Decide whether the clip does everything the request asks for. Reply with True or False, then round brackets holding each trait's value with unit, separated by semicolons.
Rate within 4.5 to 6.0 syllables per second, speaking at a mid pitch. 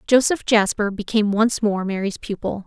False (5.1 syllables/s; 210 Hz)